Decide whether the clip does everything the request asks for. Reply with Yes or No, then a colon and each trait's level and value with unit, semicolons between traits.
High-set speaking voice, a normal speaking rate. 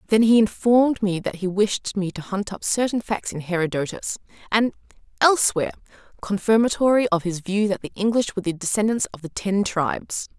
Yes: high, 205 Hz; average, 180 wpm